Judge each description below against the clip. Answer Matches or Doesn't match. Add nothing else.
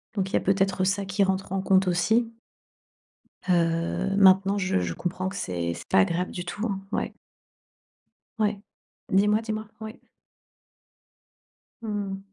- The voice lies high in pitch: Matches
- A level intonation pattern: Matches